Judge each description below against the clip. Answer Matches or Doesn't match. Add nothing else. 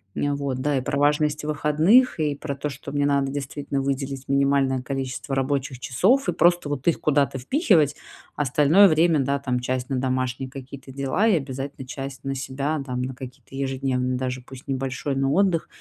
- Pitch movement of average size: Doesn't match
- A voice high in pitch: Doesn't match